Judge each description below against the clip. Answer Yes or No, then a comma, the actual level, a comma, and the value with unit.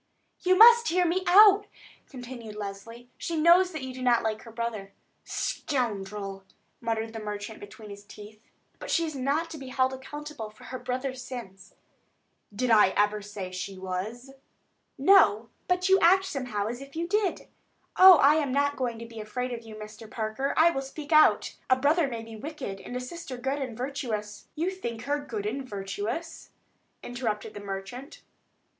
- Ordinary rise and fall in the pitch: No, wide, 5.7 semitones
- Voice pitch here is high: Yes, very high, 250 Hz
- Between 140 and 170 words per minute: No, average, 180 wpm